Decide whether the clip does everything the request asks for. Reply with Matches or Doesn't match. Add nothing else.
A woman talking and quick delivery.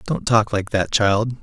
Doesn't match